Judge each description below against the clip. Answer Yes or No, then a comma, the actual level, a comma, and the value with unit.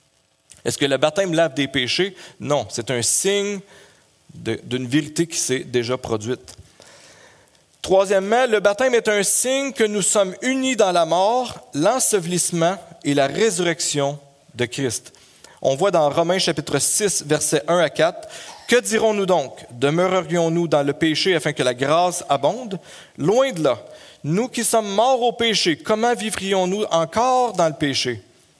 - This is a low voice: No, medium, 170 Hz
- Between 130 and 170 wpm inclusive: Yes, average, 155 wpm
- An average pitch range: No, wide, 6.6 semitones